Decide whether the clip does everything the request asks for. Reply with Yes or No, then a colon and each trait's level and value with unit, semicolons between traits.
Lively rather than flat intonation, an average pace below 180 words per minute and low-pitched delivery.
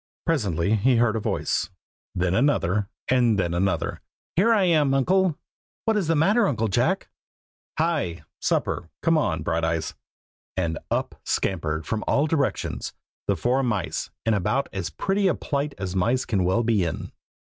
Yes: wide, 8.5 semitones; average, 160 wpm; low, 115 Hz